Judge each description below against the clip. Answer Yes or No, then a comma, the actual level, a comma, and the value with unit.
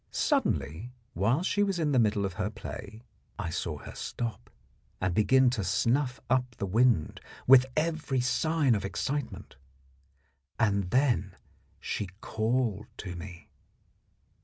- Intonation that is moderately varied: Yes, average, 5.0 semitones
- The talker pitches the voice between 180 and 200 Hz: No, low, 115 Hz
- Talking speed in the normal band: No, slow, 130 wpm